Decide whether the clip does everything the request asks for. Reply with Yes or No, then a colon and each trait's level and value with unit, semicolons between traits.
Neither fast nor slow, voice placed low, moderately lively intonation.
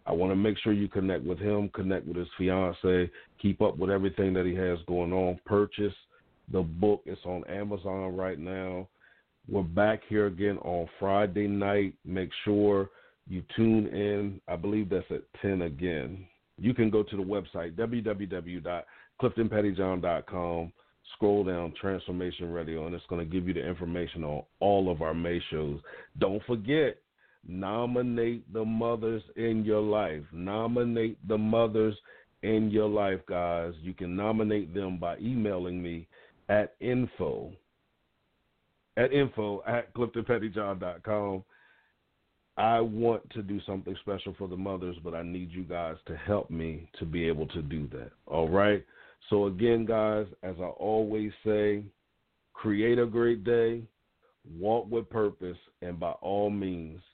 Yes: average, 150 wpm; low, 100 Hz; average, 3.2 semitones